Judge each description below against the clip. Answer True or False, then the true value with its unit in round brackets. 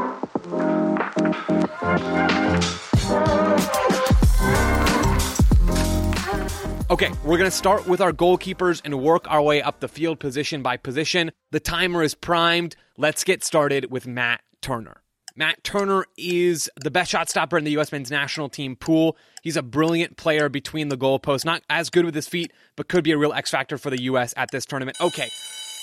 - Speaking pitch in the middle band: True (155 Hz)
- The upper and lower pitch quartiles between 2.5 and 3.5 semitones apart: True (3.2 semitones)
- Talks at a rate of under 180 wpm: True (160 wpm)